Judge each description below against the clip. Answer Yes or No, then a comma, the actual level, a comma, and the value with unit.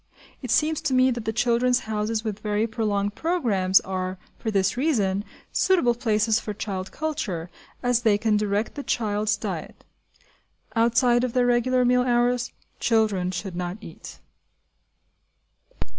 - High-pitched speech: Yes, high, 225 Hz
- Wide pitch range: No, average, 3.3 semitones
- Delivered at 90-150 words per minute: Yes, average, 145 wpm